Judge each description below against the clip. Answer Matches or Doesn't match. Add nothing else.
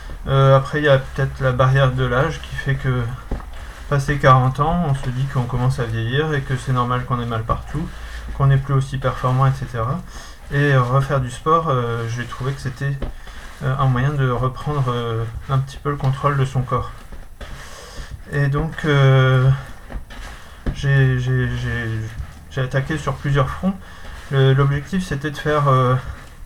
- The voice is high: Doesn't match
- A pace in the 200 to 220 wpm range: Doesn't match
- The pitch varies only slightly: Matches